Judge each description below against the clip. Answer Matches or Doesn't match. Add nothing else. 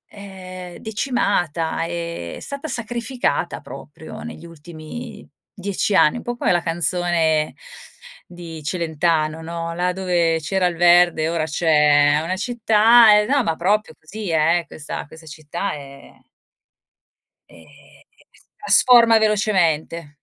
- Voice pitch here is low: Doesn't match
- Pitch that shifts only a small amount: Doesn't match